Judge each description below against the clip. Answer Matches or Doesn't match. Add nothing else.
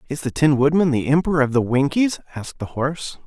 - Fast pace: Matches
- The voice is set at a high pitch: Doesn't match